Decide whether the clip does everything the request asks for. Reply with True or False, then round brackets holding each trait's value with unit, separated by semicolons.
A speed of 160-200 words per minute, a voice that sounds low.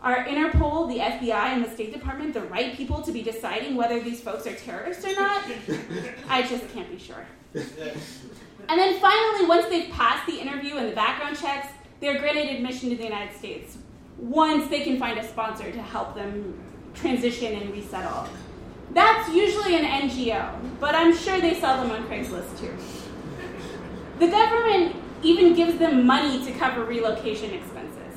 False (170 wpm; 275 Hz)